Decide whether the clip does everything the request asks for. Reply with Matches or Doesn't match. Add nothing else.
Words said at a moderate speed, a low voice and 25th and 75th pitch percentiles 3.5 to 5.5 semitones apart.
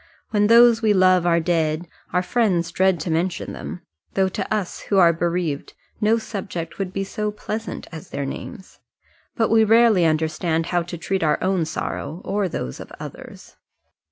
Doesn't match